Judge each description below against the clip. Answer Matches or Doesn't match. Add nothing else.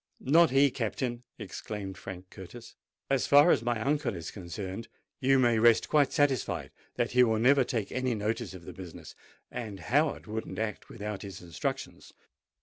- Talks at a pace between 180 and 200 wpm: Doesn't match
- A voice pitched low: Matches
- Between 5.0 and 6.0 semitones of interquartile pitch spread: Doesn't match